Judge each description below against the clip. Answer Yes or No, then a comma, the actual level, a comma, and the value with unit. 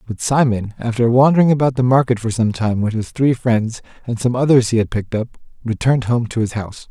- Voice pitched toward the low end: Yes, low, 120 Hz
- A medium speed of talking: No, fast, 225 wpm